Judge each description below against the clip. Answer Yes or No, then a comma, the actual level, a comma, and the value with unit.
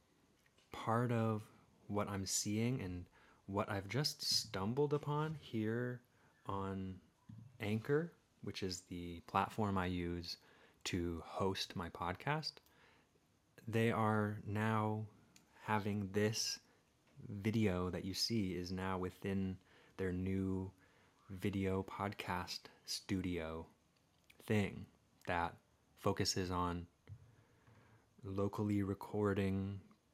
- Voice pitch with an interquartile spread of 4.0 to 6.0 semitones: No, average, 3.0 semitones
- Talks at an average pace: No, slow, 95 wpm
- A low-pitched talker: Yes, low, 100 Hz